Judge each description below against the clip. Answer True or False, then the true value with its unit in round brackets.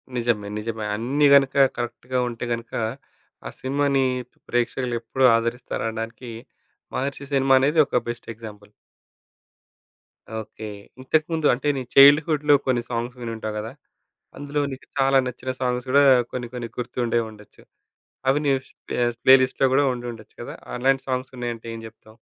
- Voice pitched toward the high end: False (125 Hz)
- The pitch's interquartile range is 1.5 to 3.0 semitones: True (2.7 semitones)